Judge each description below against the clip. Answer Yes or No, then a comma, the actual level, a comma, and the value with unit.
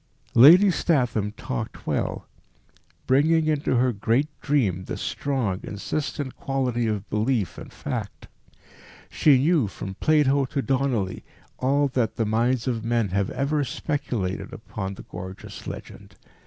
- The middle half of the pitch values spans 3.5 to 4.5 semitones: No, average, 4.9 semitones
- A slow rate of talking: Yes, slow, 130 wpm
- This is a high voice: No, low, 125 Hz